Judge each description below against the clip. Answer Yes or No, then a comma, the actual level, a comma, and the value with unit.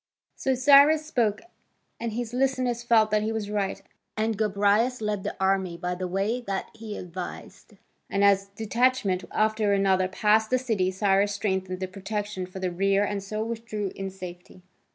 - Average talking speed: Yes, average, 175 wpm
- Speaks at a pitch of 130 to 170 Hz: No, high, 205 Hz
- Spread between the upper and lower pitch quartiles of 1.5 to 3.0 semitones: Yes, average, 2.7 semitones